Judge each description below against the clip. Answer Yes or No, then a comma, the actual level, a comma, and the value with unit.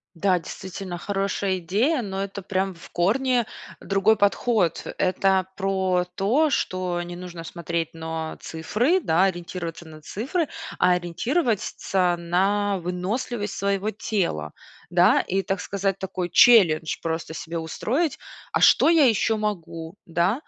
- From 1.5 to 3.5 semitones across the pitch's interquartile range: Yes, average, 3.2 semitones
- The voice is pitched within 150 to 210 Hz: Yes, high, 190 Hz